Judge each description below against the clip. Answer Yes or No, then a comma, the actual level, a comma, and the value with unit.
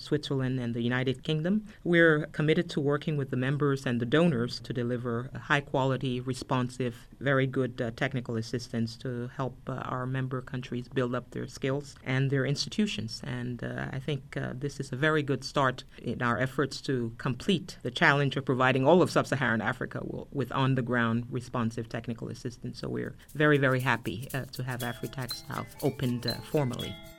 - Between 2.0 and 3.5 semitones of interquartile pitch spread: Yes, average, 2.8 semitones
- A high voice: No, low, 130 Hz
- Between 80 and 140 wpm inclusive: No, average, 185 wpm